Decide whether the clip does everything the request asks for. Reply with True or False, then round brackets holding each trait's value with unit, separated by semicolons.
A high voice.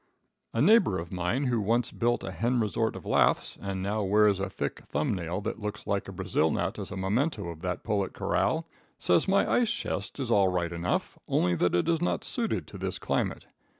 False (100 Hz)